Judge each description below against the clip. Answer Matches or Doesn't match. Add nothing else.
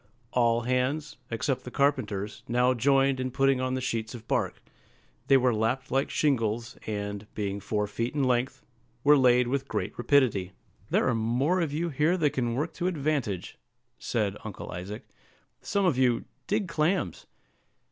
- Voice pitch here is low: Matches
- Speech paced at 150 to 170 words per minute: Matches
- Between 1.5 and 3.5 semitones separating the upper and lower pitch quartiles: Doesn't match